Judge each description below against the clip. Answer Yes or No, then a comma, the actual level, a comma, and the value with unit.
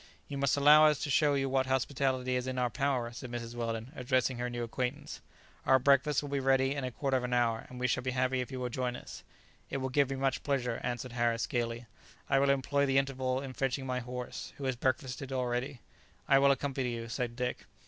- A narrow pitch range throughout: Yes, narrow, 1.8 semitones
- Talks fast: Yes, fast, 230 wpm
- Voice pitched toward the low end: Yes, low, 130 Hz